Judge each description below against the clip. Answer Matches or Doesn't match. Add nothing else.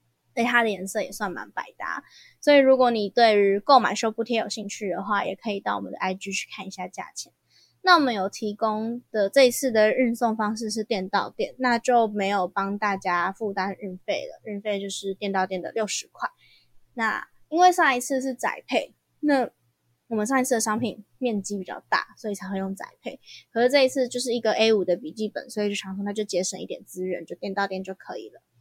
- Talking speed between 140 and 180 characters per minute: Doesn't match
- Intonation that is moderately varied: Matches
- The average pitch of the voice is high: Matches